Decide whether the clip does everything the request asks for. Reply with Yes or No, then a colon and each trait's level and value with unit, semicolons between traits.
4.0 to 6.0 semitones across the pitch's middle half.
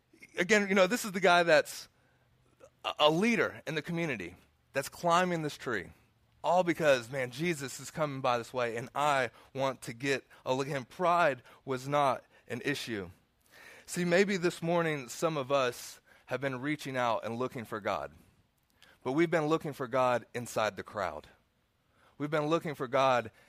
Yes: average, 5.0 semitones